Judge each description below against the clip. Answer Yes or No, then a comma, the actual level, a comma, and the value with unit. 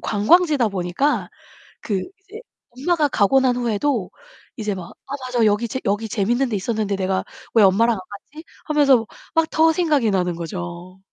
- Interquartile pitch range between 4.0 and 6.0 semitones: No, wide, 6.5 semitones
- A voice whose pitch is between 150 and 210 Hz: No, high, 225 Hz